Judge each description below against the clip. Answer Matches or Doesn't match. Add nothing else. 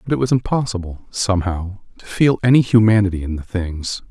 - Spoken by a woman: Doesn't match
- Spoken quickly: Doesn't match